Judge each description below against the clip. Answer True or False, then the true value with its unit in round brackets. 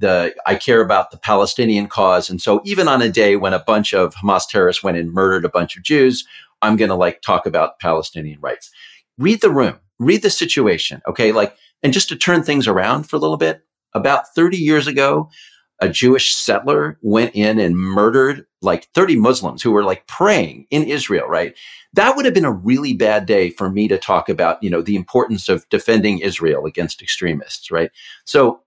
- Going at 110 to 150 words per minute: False (205 wpm)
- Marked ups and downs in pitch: True (7.0 semitones)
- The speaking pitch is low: True (105 Hz)